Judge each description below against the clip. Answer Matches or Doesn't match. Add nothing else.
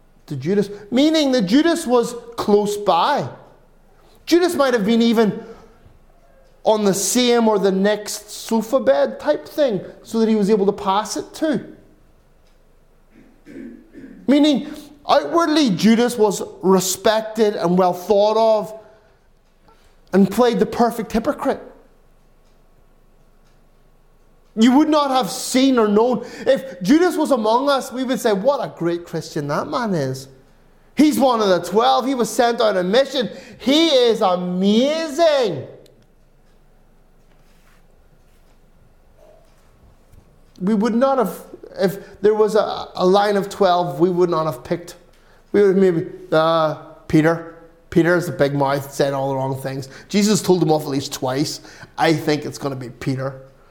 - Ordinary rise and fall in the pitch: Doesn't match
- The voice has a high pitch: Matches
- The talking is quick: Doesn't match